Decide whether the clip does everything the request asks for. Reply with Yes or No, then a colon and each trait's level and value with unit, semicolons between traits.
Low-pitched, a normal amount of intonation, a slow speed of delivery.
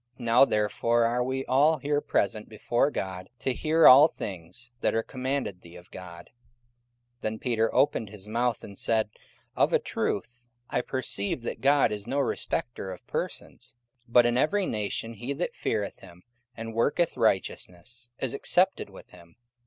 No: low, 115 Hz; average, 4.2 semitones; average, 170 wpm